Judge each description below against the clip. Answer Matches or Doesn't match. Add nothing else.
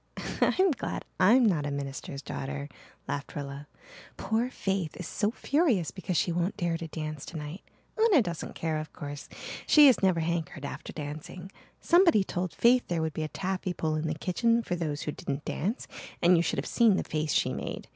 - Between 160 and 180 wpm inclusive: Doesn't match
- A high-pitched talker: Doesn't match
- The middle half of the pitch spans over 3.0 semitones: Matches